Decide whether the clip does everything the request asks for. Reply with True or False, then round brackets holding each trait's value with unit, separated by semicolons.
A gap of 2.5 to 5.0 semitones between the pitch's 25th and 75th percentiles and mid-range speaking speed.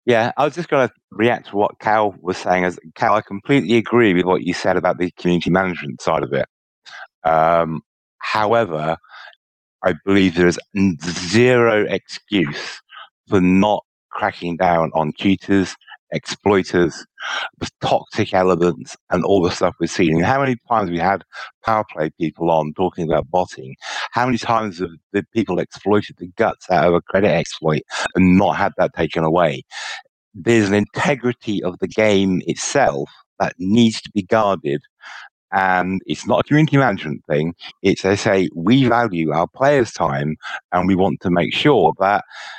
True (3.8 semitones; 170 wpm)